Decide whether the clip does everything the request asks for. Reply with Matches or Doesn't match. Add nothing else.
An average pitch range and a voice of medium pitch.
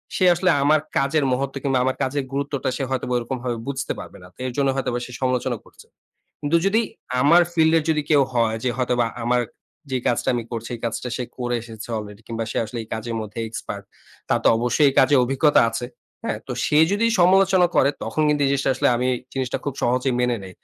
Doesn't match